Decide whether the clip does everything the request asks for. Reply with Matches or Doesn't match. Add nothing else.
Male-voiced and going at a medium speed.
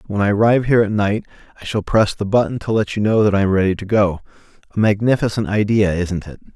Doesn't match